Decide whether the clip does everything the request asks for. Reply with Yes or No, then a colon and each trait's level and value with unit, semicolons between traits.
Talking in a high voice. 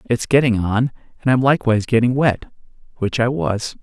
No: low, 120 Hz